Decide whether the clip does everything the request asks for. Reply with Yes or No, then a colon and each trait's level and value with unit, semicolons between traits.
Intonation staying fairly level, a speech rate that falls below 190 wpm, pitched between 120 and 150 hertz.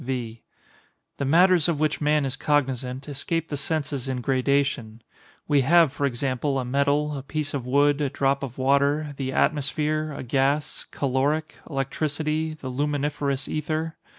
Yes: narrow, 2.2 semitones; average, 150 wpm; medium, 140 Hz